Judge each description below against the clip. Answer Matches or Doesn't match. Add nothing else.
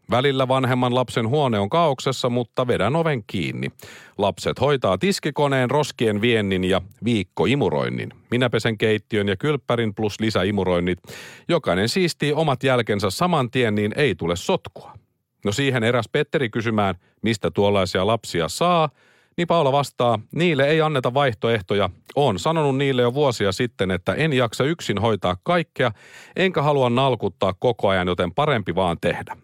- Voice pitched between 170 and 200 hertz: Doesn't match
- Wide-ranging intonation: Matches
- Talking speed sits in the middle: Matches